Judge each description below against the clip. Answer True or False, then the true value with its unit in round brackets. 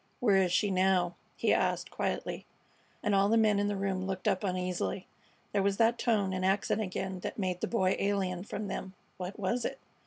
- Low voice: False (195 Hz)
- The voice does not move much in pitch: True (1.8 semitones)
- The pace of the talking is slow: False (205 wpm)